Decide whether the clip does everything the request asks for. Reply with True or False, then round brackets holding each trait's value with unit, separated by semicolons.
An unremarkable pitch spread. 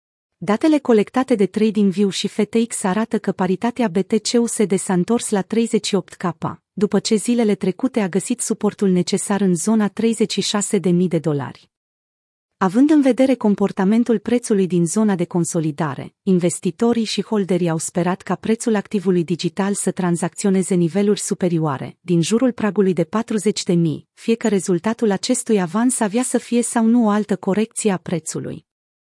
True (3.5 semitones)